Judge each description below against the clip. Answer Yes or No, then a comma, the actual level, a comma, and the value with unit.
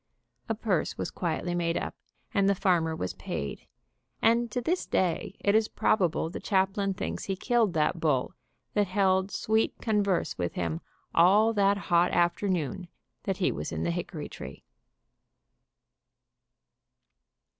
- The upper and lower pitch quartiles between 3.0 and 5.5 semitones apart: Yes, average, 3.5 semitones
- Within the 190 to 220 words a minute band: No, average, 145 wpm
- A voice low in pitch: No, medium, 185 Hz